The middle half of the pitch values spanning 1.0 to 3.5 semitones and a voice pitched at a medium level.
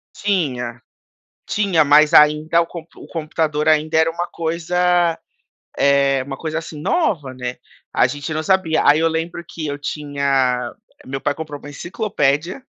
Yes: average, 2.9 semitones; medium, 155 Hz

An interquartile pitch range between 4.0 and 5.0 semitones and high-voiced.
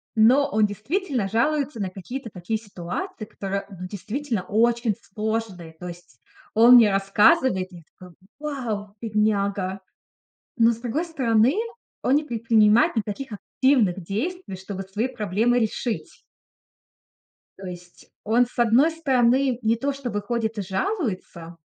Yes: average, 4.3 semitones; high, 220 Hz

